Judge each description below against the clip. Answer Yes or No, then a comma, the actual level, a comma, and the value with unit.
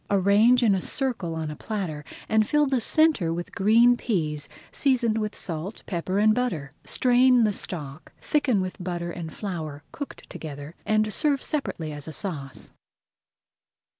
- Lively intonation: Yes, wide, 6.8 semitones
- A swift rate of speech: No, average, 155 wpm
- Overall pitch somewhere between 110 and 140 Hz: No, high, 200 Hz